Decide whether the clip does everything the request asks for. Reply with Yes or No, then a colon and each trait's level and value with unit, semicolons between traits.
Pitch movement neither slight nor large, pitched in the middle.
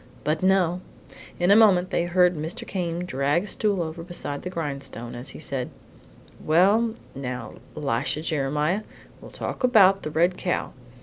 Yes: average, 4.0 semitones; medium, 170 Hz